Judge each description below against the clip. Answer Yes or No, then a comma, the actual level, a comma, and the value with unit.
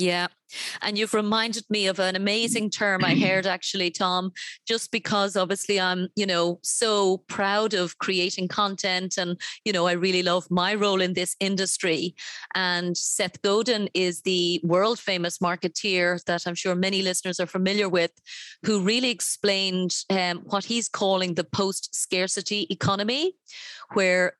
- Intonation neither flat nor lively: No, narrow, 2.2 semitones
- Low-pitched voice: No, high, 190 Hz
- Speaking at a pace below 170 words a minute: Yes, average, 155 wpm